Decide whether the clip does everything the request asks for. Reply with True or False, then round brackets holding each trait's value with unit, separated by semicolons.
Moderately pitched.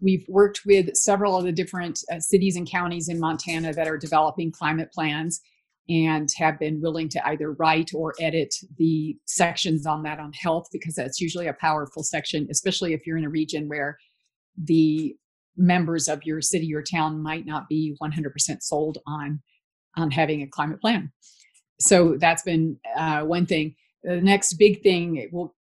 True (160 Hz)